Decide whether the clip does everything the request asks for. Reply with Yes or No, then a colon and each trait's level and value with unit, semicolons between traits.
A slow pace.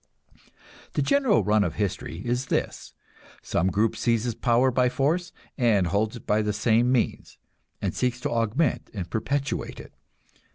No: average, 155 wpm